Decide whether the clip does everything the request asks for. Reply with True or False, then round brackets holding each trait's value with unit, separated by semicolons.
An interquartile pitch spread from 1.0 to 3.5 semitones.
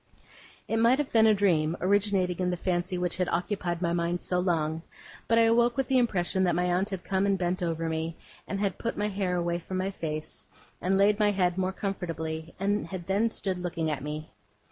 True (2.8 semitones)